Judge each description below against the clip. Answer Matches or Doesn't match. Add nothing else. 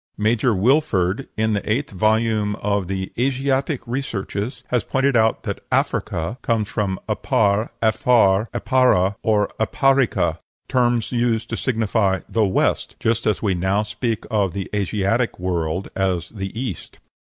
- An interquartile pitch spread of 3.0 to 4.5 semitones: Matches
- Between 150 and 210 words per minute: Doesn't match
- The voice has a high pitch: Doesn't match